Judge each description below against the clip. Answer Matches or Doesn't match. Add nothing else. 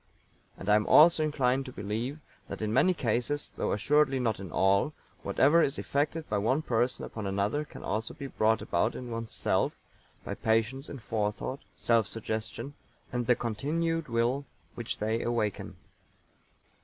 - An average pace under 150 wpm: Doesn't match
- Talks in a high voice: Doesn't match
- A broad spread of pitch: Doesn't match